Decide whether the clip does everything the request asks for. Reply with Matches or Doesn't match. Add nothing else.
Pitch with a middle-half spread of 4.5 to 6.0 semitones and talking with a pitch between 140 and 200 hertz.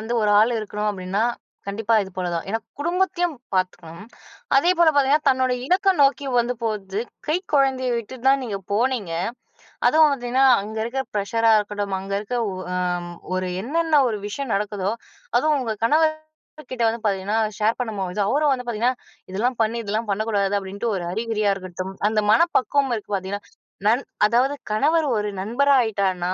Doesn't match